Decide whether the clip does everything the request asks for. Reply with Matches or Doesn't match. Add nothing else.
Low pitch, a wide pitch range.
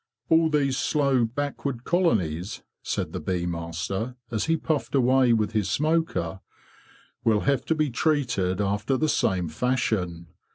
Matches